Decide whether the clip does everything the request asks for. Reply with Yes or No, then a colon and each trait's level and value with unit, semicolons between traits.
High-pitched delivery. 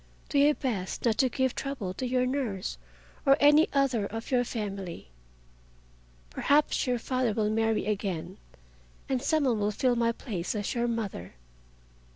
Yes: high, 235 Hz